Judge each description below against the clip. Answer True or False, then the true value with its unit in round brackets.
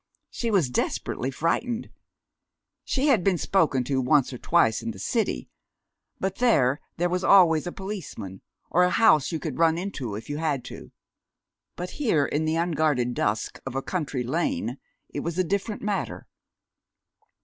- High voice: False (160 Hz)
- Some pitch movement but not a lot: False (5.9 semitones)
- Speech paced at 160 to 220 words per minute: True (165 wpm)